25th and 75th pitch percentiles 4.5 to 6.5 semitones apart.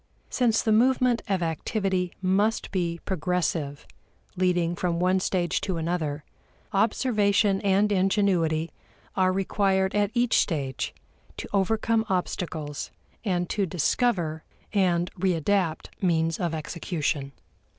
No: average, 3.3 semitones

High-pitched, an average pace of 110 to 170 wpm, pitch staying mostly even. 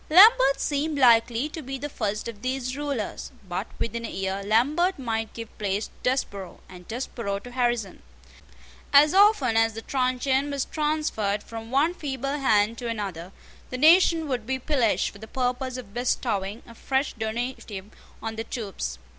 No: high, 245 Hz; average, 165 wpm; average, 4.1 semitones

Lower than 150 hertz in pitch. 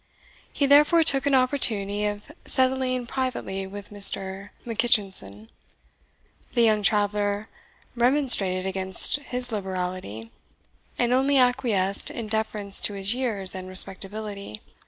No: high, 210 Hz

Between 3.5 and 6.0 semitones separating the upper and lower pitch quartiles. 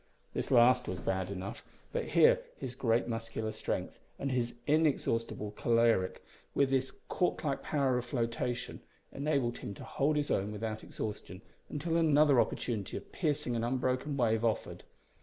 Yes: average, 3.8 semitones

